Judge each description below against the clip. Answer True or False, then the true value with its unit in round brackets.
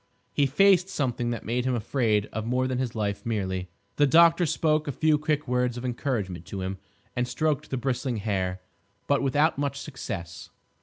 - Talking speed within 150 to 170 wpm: False (185 wpm)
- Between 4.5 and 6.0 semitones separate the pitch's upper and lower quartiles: True (5.1 semitones)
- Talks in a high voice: False (125 Hz)